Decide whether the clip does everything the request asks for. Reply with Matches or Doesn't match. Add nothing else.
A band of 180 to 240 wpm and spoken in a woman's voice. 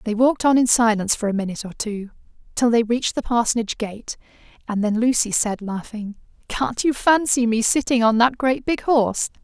Matches